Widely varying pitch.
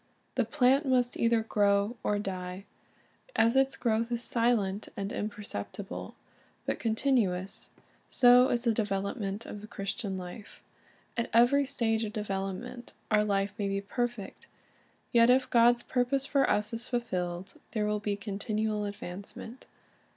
No: average, 3.3 semitones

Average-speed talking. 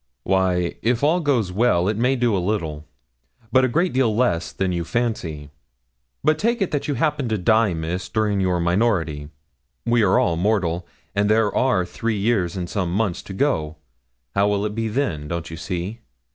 Yes: average, 190 wpm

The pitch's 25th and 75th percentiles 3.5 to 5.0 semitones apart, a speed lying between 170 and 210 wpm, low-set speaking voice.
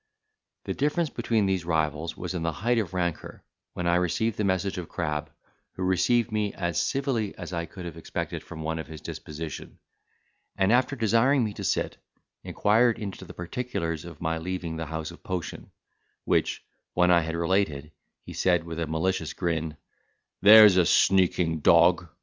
Yes: average, 3.9 semitones; average, 175 wpm; very low, 90 Hz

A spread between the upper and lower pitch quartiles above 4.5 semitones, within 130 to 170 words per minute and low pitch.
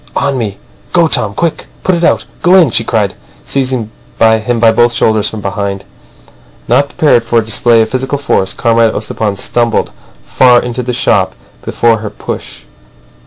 No: average, 2.8 semitones; average, 165 wpm; low, 115 Hz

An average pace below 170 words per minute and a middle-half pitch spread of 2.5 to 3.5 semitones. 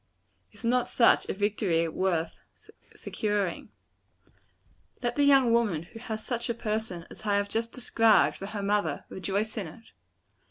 Yes: average, 155 wpm; average, 3.2 semitones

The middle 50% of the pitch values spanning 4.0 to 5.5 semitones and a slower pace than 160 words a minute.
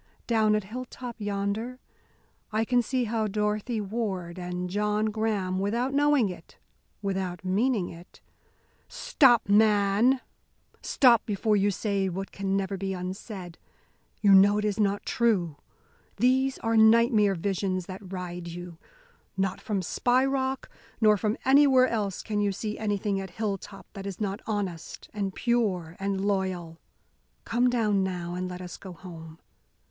No: average, 3.0 semitones; average, 150 wpm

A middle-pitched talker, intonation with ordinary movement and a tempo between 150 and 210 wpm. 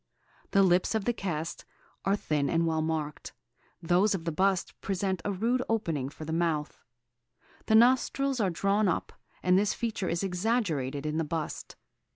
Yes: medium, 180 Hz; average, 4.3 semitones; average, 170 wpm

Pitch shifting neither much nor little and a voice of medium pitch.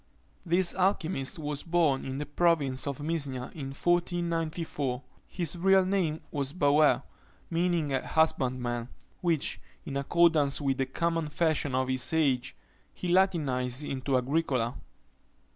Yes: average, 4.1 semitones; medium, 150 Hz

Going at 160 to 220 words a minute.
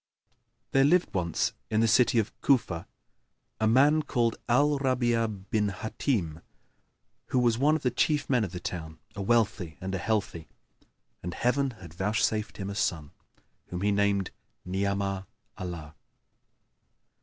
No: average, 145 wpm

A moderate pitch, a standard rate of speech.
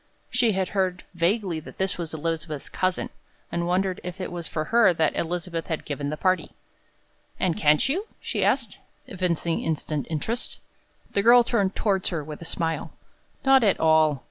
Yes: medium, 175 Hz; average, 170 wpm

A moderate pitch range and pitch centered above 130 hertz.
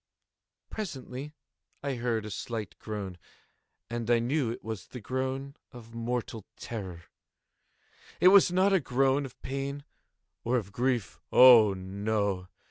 No: average, 3.9 semitones; low, 120 Hz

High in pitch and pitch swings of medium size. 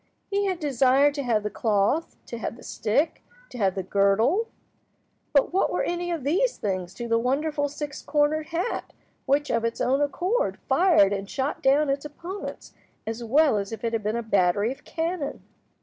No: very high, 275 Hz; wide, 5.8 semitones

